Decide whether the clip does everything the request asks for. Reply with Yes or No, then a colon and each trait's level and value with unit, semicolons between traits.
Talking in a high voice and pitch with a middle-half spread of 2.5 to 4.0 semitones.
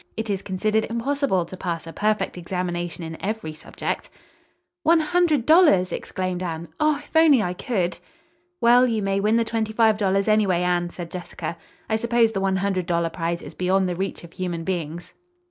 No: high, 195 Hz; average, 4.4 semitones